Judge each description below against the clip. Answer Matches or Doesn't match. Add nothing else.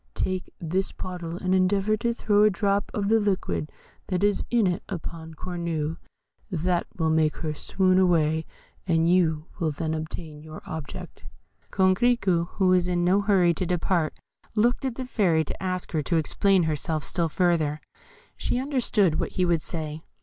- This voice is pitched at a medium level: Matches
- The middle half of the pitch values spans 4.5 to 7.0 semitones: Doesn't match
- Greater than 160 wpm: Matches